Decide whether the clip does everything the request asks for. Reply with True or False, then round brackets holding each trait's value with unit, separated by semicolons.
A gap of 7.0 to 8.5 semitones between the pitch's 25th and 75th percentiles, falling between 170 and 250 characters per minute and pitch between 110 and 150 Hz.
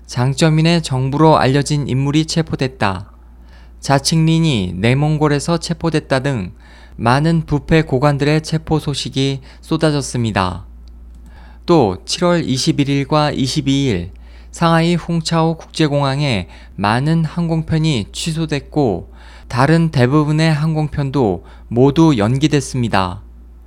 True (7.3 semitones; 240 characters per minute; 140 Hz)